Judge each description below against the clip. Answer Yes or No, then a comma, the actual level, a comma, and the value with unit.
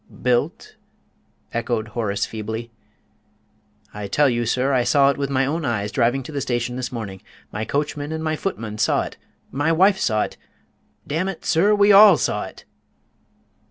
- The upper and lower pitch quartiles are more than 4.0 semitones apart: Yes, average, 5.3 semitones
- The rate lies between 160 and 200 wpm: Yes, average, 165 wpm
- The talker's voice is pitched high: No, low, 130 Hz